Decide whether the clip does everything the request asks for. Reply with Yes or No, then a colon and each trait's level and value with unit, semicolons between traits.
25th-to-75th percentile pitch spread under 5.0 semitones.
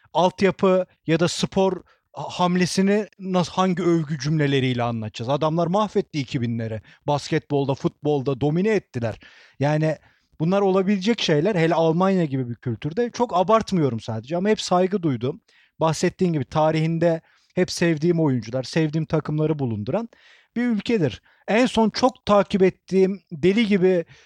Yes: average, 4.6 semitones